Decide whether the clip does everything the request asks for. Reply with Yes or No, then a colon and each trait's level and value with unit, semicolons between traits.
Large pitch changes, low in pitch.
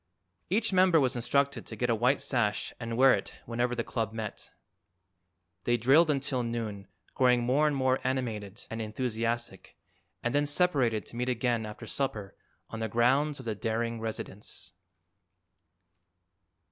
No: average, 3.0 semitones; low, 120 Hz